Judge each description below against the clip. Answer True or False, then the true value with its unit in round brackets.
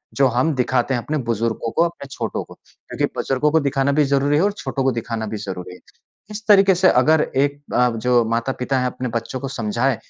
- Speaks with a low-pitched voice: True (130 Hz)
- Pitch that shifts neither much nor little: True (3.5 semitones)